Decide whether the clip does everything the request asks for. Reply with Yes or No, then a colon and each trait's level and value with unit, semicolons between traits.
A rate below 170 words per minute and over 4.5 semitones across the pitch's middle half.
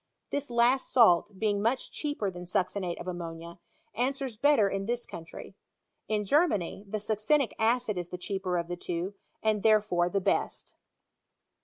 Yes: average, 155 wpm; average, 4.9 semitones